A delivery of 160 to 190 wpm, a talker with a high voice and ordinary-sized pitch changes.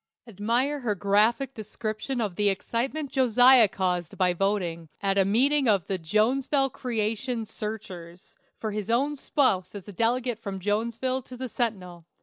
No: average, 150 wpm; high, 220 Hz; average, 4.3 semitones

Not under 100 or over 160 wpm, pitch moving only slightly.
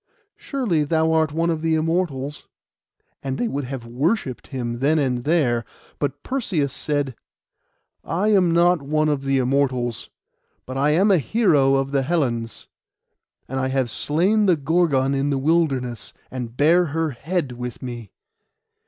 No: average, 155 wpm; average, 3.9 semitones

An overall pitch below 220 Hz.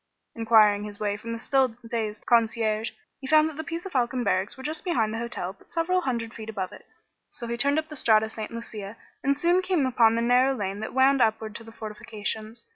No: high, 230 Hz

